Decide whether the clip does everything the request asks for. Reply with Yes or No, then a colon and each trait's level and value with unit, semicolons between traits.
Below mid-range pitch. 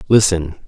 Yes: very low, 90 Hz